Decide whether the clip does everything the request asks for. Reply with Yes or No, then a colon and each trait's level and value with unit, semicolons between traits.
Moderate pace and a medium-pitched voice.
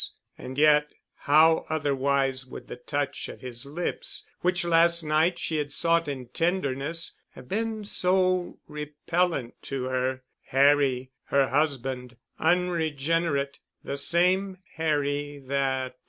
No: slow, 110 wpm; medium, 145 Hz